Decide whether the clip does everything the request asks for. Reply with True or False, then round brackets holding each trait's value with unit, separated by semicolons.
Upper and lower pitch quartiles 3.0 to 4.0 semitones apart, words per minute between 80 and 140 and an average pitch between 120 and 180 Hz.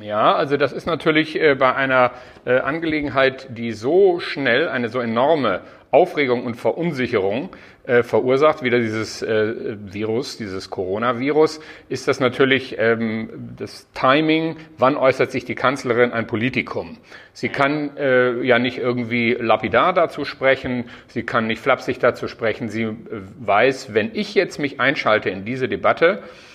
True (3.5 semitones; 135 wpm; 125 Hz)